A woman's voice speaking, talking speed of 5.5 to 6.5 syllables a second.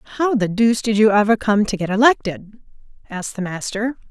Yes: female; 6.2 syllables/s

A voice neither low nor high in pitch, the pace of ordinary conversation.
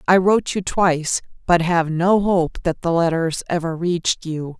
Yes: medium, 170 Hz; average, 185 wpm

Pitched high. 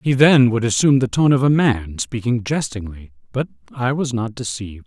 No: low, 120 Hz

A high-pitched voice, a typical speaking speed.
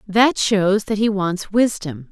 Yes: high, 200 Hz; average, 170 wpm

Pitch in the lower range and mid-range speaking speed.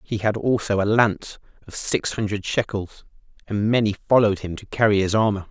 Yes: low, 105 Hz; average, 185 wpm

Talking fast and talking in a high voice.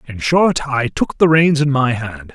No: fast, 230 wpm; low, 135 Hz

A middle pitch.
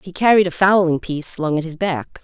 Yes: medium, 170 Hz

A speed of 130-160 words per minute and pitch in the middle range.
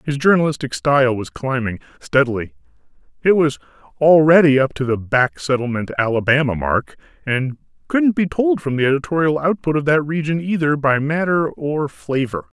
Yes: average, 155 wpm; medium, 145 Hz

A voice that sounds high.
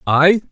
No: medium, 165 Hz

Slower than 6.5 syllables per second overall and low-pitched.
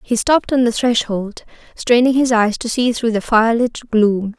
No: 4.5 syllables/s; high, 230 Hz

